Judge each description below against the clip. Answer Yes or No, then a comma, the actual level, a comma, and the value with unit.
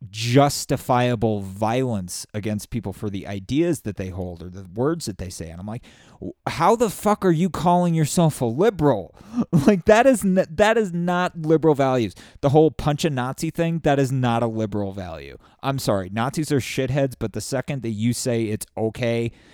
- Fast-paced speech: No, average, 190 wpm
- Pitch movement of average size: No, wide, 6.8 semitones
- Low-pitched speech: Yes, low, 130 Hz